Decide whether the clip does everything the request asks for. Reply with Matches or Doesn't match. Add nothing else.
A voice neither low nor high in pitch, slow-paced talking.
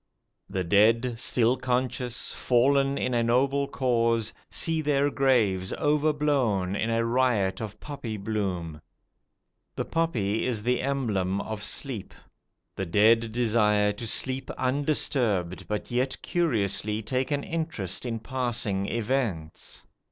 Doesn't match